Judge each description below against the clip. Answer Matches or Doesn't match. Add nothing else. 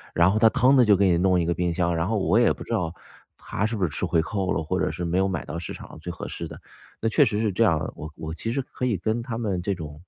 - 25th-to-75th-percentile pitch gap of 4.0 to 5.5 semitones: Matches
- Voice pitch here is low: Matches